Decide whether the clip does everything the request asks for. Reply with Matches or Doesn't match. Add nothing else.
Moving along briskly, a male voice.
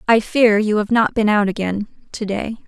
Doesn't match